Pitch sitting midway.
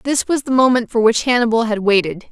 No: high, 235 Hz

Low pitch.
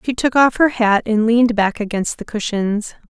No: high, 220 Hz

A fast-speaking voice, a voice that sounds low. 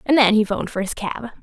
No: fast, 295 wpm; high, 220 Hz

